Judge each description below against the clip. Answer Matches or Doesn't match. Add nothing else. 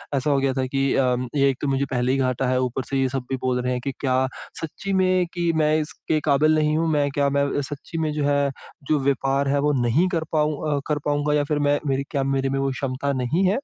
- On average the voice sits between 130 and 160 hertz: Matches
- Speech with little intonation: Matches